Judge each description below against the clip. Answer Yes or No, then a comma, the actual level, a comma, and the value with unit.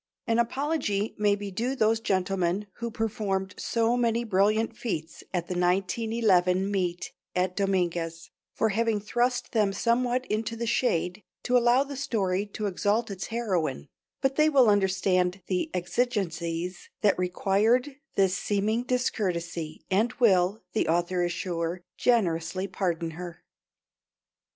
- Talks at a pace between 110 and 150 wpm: Yes, slow, 135 wpm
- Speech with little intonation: No, average, 4.3 semitones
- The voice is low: No, high, 200 Hz